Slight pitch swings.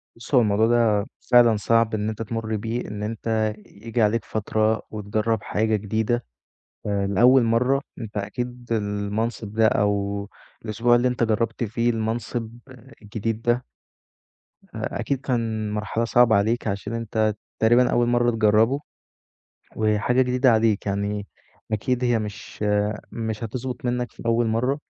Yes: narrow, 2.2 semitones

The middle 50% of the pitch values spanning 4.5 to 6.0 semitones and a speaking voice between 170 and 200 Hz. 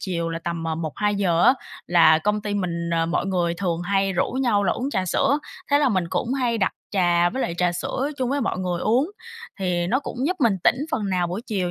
Yes: average, 5.1 semitones; high, 190 Hz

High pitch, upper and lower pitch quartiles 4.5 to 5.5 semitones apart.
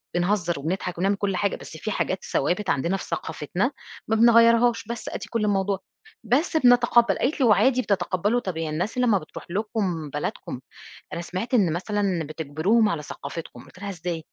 Yes: high, 195 Hz; average, 5.0 semitones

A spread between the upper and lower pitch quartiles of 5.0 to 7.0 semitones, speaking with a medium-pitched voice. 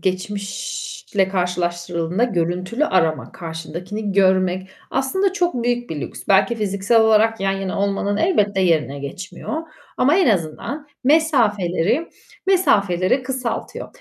No: average, 5.3 semitones; high, 200 Hz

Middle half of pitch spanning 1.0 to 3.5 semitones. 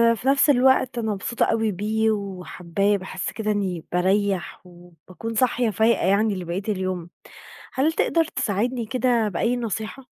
No: average, 4.1 semitones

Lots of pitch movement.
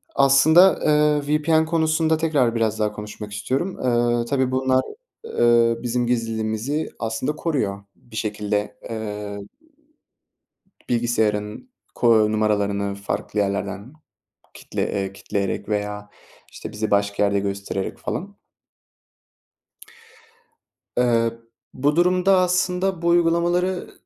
Yes: wide, 6.7 semitones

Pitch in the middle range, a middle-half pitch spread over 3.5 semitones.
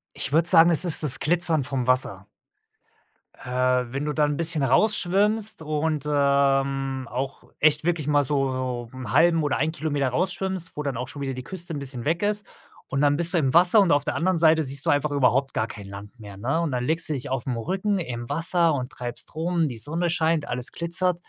Yes: medium, 150 Hz; average, 4.2 semitones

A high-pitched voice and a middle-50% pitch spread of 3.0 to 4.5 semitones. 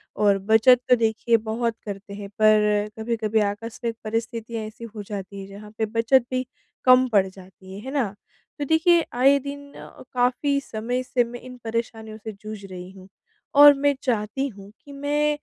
Yes: high, 225 Hz; average, 3.4 semitones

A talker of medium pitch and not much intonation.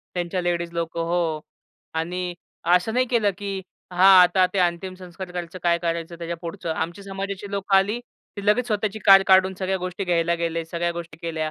Yes: medium, 180 Hz; narrow, 2.3 semitones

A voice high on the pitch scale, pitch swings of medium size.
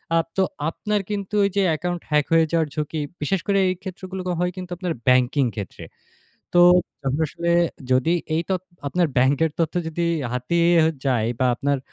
No: medium, 165 Hz; average, 4.4 semitones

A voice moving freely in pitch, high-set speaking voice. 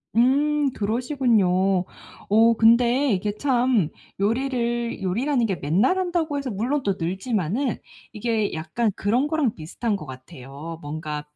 Yes: wide, 5.8 semitones; high, 225 Hz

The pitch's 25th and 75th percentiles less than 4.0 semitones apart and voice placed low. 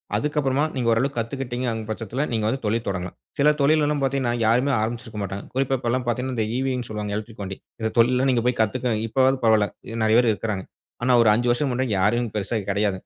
Yes: average, 3.1 semitones; low, 120 Hz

